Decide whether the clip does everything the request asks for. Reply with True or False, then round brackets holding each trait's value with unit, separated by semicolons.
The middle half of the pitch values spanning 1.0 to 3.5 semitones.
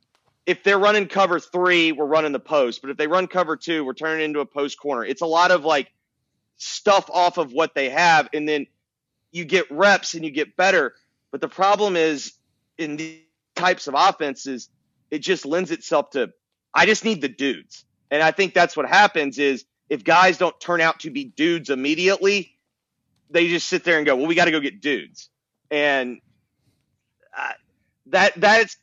False (4.2 semitones)